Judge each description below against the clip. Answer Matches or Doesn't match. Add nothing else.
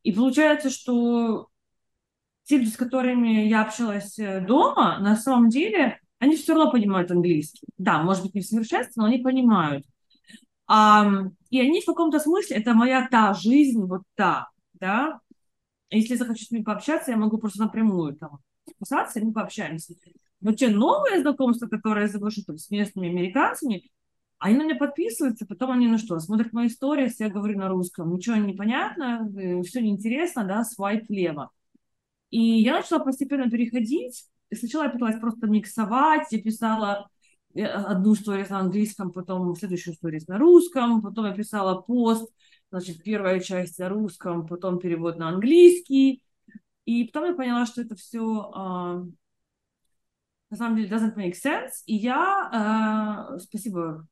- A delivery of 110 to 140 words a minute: Doesn't match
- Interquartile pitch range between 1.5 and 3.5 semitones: Doesn't match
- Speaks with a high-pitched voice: Matches